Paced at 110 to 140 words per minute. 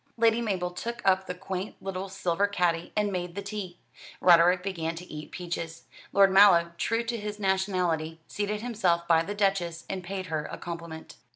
No: average, 180 wpm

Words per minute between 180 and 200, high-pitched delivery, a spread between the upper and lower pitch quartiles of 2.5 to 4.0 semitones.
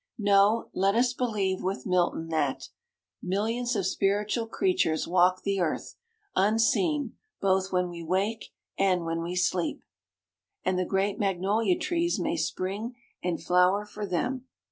No: average, 140 wpm; high, 195 Hz; average, 3.7 semitones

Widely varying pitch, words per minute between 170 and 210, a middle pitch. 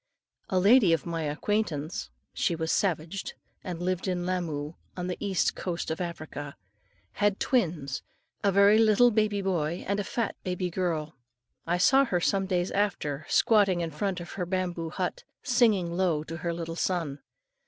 No: average, 3.3 semitones; average, 175 wpm; medium, 180 Hz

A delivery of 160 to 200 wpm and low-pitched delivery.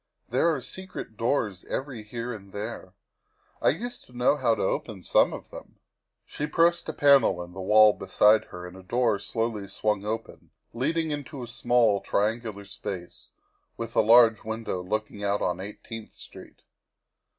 Yes: average, 175 wpm; low, 110 Hz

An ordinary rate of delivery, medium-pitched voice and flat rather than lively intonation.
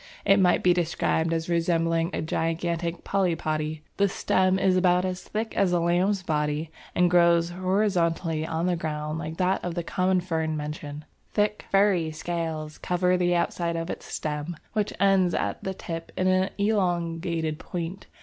Yes: average, 165 wpm; medium, 170 Hz; narrow, 2.2 semitones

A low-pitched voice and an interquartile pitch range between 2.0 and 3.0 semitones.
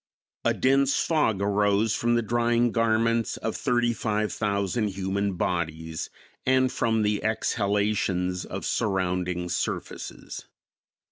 No: low, 105 Hz; average, 3.5 semitones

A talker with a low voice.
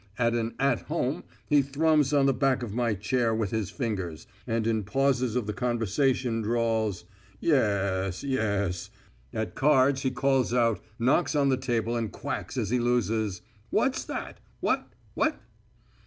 Yes: low, 120 Hz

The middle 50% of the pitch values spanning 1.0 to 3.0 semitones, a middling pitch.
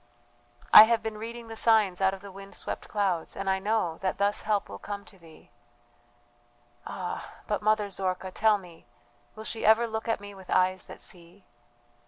No: average, 2.7 semitones; high, 200 Hz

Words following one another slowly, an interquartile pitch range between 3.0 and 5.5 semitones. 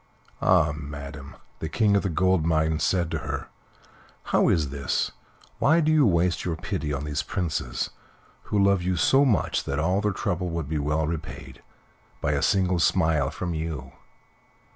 No: average, 170 wpm; average, 3.7 semitones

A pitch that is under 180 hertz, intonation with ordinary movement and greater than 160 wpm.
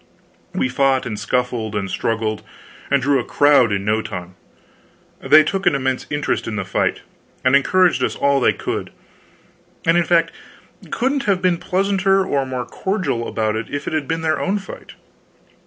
No: medium, 140 Hz; wide, 6.9 semitones; average, 170 wpm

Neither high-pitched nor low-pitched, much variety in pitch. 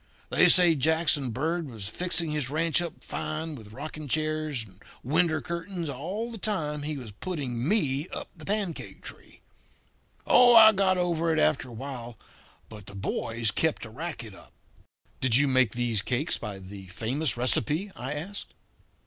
Yes: medium, 150 Hz; wide, 5.7 semitones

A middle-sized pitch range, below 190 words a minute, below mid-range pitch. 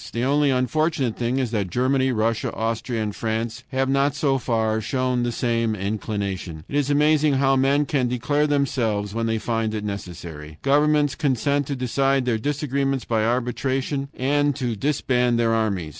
Yes: average, 3.8 semitones; average, 170 wpm; low, 125 Hz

